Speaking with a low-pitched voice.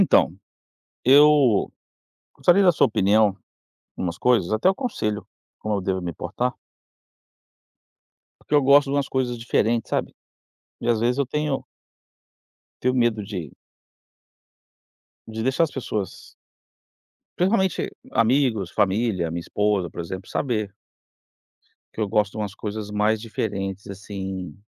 Yes: low, 110 Hz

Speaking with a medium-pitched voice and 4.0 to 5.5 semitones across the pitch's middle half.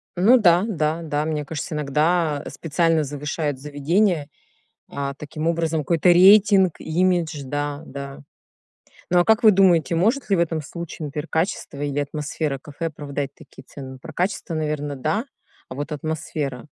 No: medium, 155 Hz; average, 3.0 semitones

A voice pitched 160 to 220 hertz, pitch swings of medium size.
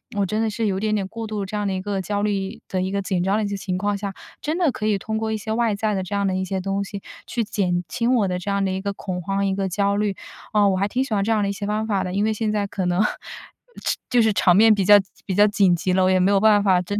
No: high, 200 Hz; narrow, 1.9 semitones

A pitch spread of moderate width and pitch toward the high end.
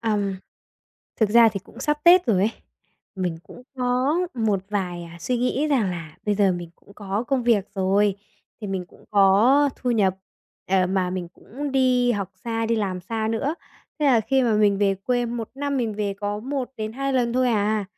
Yes: average, 4.1 semitones; high, 220 Hz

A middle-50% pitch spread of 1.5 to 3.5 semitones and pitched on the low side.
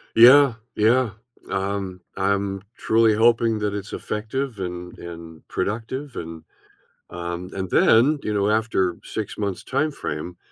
No: average, 3.9 semitones; low, 105 Hz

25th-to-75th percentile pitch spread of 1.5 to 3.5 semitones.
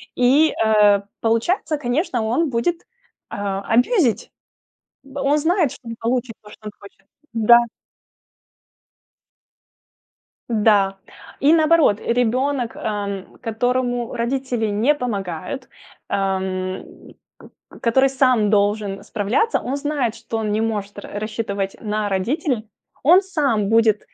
No: average, 4.4 semitones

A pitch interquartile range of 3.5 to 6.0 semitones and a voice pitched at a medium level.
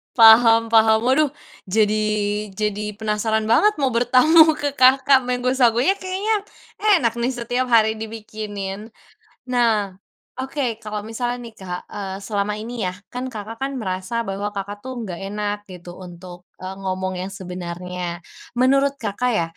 No: average, 4.0 semitones; high, 220 Hz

